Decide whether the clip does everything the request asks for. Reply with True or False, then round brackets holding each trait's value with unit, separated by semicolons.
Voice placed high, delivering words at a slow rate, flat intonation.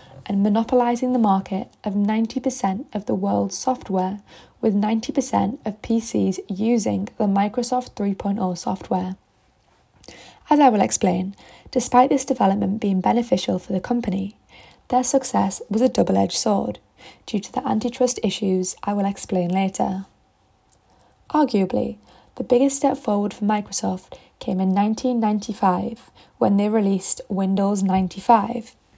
False (210 Hz; 130 wpm; 4.2 semitones)